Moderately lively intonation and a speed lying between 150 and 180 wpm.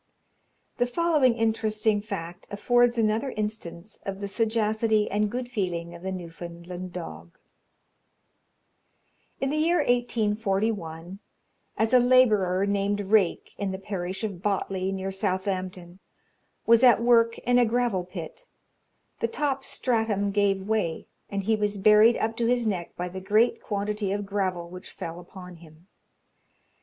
No: average, 3.6 semitones; average, 140 wpm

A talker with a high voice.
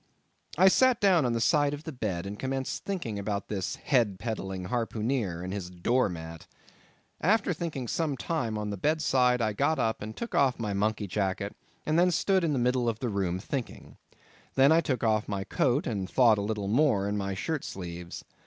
No: low, 115 Hz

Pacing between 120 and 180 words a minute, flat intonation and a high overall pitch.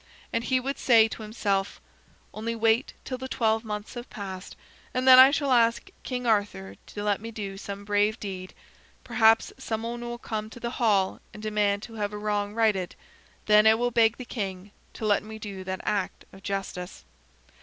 No: average, 195 wpm; narrow, 2.3 semitones; high, 215 Hz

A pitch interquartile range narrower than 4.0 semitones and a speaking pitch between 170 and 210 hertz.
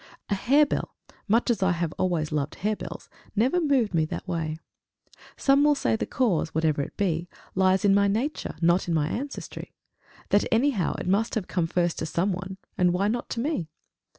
No: average, 5.2 semitones; high, 190 Hz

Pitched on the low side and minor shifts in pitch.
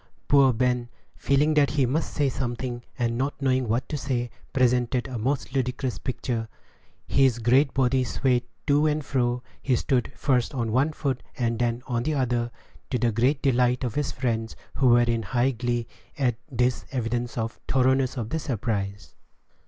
Yes: low, 125 Hz; narrow, 2.1 semitones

